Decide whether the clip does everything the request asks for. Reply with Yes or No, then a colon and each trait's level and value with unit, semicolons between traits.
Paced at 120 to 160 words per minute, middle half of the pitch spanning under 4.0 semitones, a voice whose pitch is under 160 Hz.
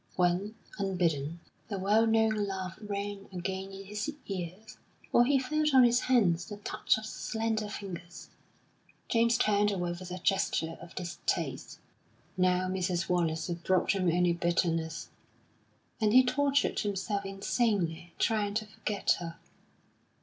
No: average, 140 wpm; average, 3.5 semitones; high, 195 Hz